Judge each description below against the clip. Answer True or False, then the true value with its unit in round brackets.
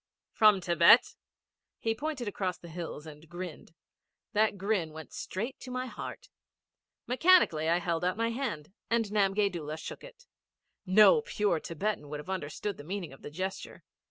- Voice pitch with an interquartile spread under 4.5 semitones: False (5.1 semitones)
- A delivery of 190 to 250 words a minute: False (160 wpm)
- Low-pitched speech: False (190 Hz)